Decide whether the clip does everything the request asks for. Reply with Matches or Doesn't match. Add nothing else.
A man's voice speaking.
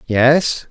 Matches